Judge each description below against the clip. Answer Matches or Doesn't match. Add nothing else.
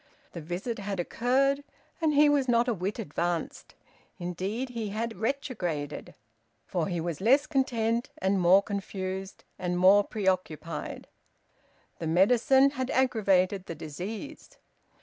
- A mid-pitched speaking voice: Doesn't match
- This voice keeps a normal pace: Doesn't match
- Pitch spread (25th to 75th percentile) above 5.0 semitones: Matches